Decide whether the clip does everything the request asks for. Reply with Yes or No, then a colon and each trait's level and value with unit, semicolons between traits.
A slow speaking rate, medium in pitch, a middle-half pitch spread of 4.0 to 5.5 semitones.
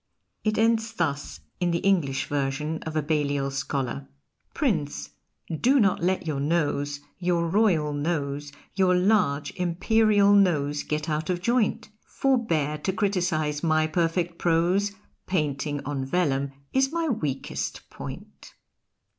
Yes: slow, 130 wpm; medium, 165 Hz; average, 5.1 semitones